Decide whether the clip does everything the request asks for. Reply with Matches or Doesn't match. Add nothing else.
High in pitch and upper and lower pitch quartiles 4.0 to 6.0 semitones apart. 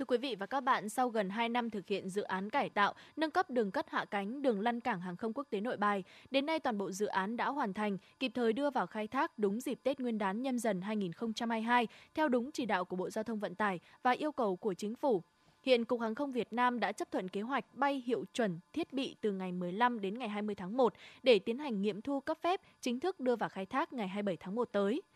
Matches